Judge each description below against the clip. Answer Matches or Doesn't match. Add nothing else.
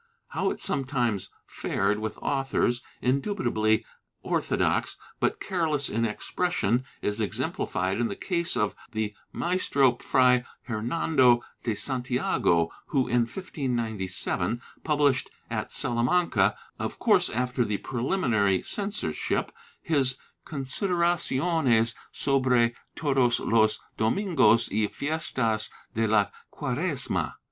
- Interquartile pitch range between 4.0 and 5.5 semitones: Matches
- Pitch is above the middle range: Doesn't match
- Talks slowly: Matches